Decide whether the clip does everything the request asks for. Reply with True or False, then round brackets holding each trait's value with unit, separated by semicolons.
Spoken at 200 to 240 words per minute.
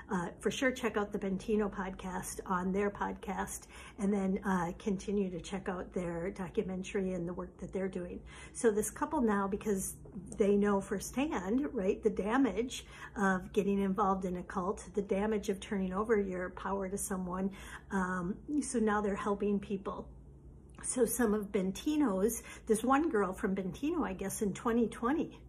False (165 wpm)